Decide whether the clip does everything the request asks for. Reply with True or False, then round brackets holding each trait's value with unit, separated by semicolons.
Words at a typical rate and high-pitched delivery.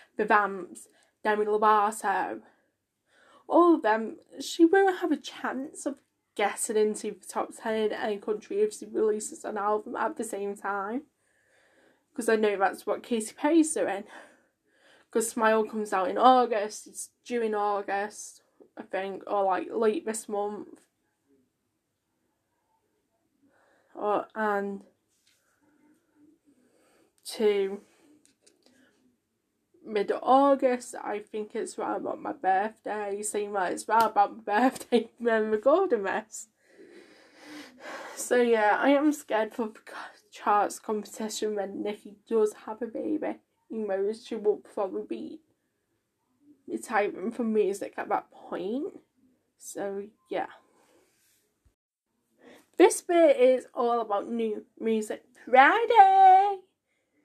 False (120 wpm; 230 Hz)